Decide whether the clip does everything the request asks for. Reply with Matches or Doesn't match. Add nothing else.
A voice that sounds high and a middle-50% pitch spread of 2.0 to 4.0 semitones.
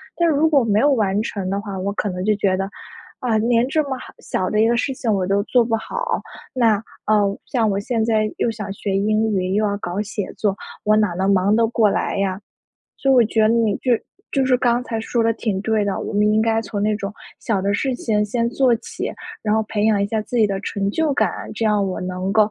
Matches